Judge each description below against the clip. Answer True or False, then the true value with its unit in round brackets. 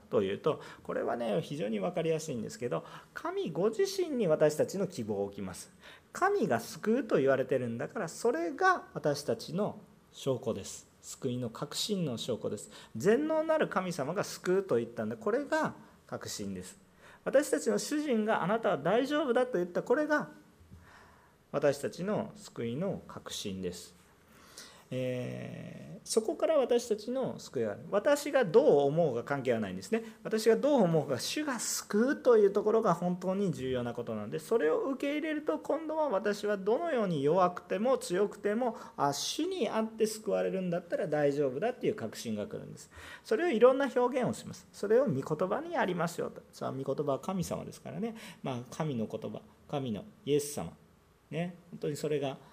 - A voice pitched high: True (205 Hz)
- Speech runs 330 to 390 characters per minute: True (345 characters per minute)